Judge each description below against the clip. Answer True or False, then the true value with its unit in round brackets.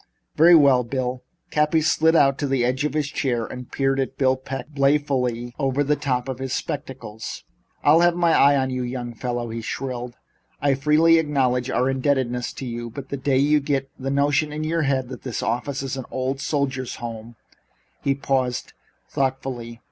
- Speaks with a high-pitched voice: False (135 Hz)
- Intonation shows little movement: True (2.3 semitones)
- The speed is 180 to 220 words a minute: True (190 wpm)